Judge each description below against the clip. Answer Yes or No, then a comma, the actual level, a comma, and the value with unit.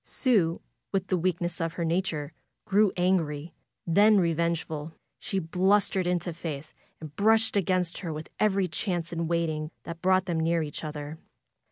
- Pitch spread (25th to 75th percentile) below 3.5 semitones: Yes, average, 2.7 semitones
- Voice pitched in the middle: Yes, medium, 170 Hz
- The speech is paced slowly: No, average, 160 wpm